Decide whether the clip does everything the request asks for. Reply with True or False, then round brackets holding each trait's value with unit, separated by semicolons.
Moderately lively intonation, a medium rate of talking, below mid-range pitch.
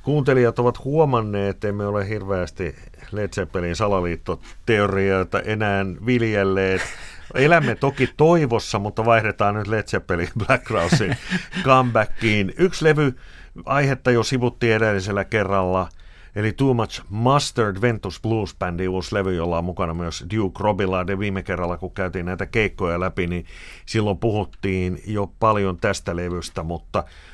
True (3.8 semitones; 130 wpm; 100 Hz)